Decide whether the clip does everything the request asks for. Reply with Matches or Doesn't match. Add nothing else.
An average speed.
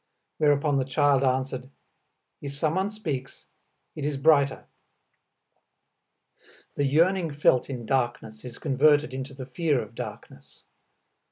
Doesn't match